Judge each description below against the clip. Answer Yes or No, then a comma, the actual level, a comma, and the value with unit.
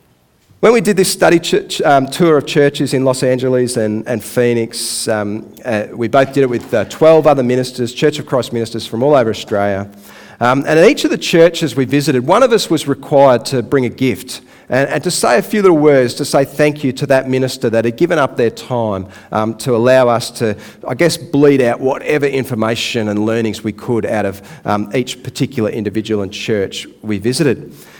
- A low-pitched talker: Yes, low, 130 Hz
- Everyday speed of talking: No, fast, 210 wpm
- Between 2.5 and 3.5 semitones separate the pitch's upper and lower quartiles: No, average, 4.3 semitones